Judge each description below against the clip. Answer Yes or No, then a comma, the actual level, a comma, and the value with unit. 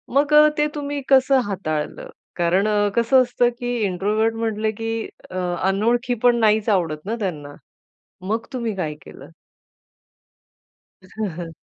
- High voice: Yes, high, 220 Hz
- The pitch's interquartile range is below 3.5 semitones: No, average, 4.7 semitones